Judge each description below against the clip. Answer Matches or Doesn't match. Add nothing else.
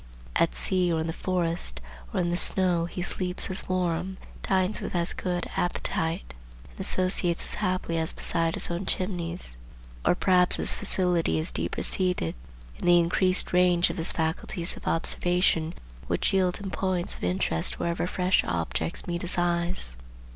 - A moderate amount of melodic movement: Doesn't match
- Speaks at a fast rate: Doesn't match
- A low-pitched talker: Doesn't match